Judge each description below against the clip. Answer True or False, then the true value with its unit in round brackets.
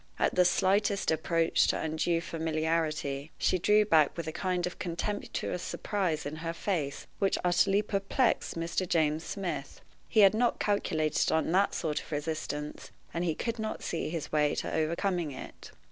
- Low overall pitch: False (170 Hz)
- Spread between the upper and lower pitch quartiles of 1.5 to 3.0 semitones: False (3.7 semitones)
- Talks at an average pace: True (165 wpm)